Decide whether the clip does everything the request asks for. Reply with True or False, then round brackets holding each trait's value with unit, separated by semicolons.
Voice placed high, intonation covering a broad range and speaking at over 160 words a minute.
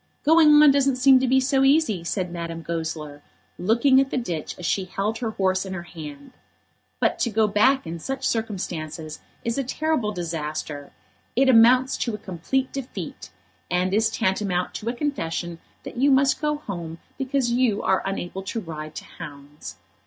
True (210 Hz; 7.6 semitones; 175 wpm)